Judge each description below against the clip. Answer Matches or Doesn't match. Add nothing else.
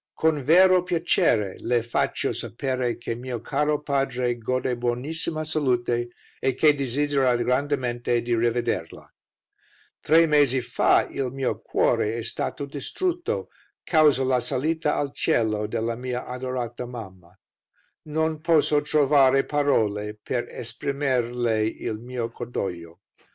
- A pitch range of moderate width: Matches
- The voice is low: Matches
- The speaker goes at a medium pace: Doesn't match